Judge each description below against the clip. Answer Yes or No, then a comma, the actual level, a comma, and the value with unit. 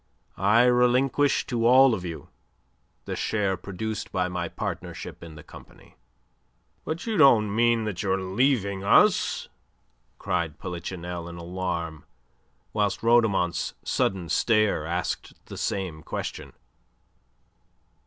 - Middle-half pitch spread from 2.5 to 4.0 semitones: No, average, 5.0 semitones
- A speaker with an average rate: No, slow, 120 wpm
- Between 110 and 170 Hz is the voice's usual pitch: No, very low, 95 Hz